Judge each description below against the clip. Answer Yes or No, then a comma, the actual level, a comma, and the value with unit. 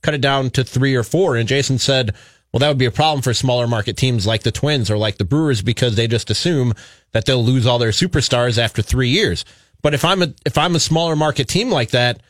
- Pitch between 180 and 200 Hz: No, low, 125 Hz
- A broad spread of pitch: No, average, 3.8 semitones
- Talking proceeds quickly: Yes, fast, 255 wpm